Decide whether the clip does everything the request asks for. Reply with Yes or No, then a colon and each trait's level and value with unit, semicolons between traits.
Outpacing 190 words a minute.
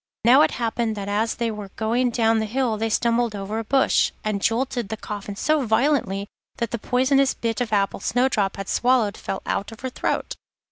Yes: average, 200 wpm